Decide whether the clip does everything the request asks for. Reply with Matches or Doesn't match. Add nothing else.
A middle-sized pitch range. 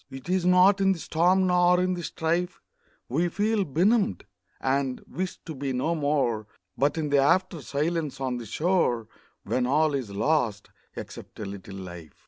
Doesn't match